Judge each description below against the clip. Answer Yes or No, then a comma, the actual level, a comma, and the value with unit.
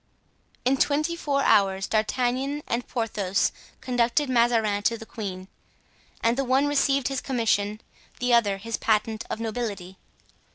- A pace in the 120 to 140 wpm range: Yes, slow, 135 wpm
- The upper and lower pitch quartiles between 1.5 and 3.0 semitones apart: No, average, 3.7 semitones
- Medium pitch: No, high, 235 Hz